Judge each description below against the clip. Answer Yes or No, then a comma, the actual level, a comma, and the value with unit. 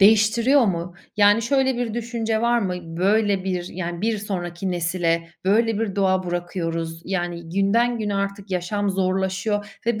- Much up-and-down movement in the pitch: No, average, 3.8 semitones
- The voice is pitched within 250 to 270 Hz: No, high, 195 Hz